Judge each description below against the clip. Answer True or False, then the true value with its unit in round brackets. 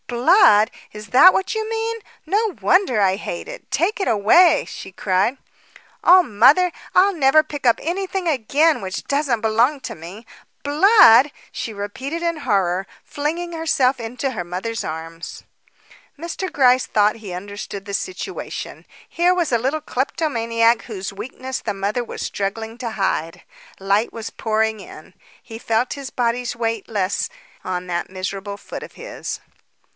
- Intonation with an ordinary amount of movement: False (7.4 semitones)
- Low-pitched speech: False (235 Hz)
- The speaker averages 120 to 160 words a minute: True (150 wpm)